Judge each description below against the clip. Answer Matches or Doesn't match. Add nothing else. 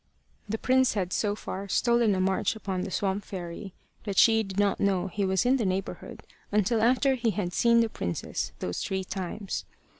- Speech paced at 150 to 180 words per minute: Doesn't match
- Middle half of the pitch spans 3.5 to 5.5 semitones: Doesn't match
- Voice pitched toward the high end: Matches